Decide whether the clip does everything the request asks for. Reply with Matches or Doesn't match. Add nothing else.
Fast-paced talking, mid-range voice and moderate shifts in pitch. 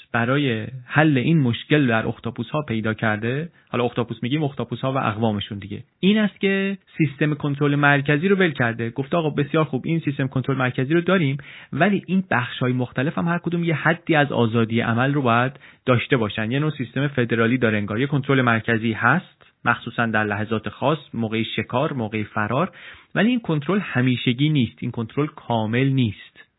Doesn't match